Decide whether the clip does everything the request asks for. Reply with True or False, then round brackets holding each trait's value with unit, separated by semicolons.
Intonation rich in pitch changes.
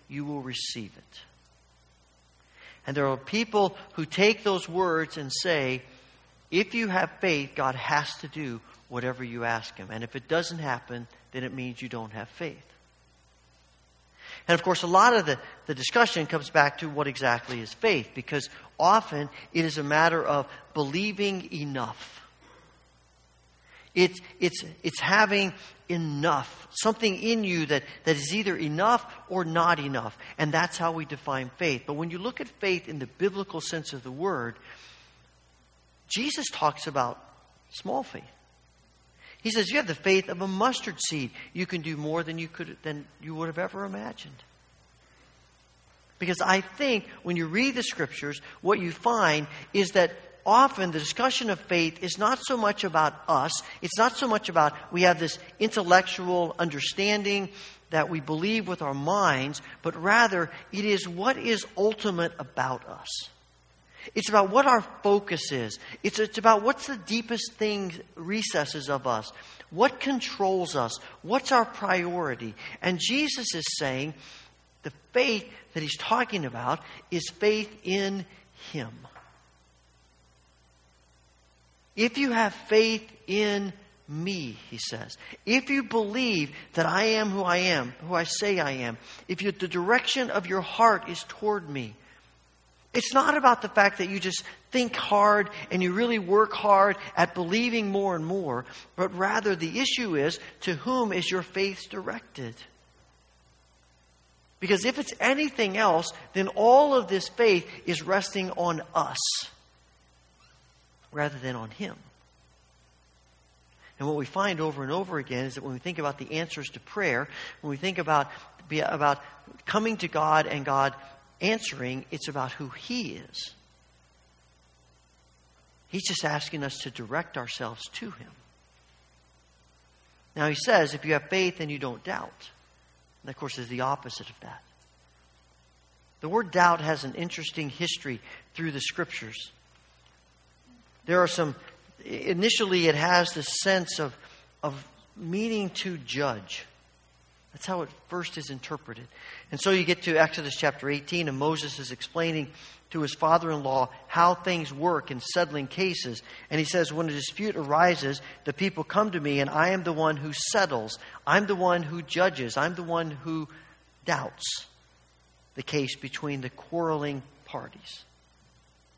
True (7.4 semitones)